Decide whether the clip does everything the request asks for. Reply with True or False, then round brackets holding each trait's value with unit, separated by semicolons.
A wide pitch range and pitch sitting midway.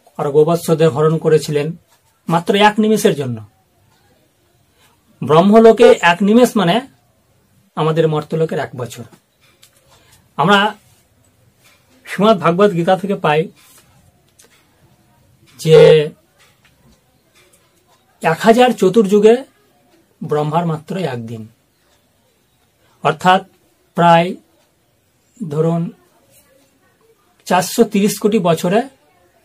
True (5.8 semitones; 170 Hz)